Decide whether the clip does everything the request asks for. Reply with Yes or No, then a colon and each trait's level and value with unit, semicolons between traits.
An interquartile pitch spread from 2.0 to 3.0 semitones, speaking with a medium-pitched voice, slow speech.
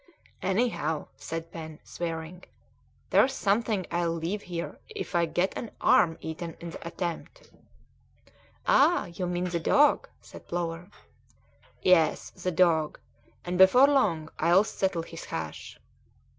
Yes: narrow, 2.5 semitones; medium, 175 Hz; slow, 130 wpm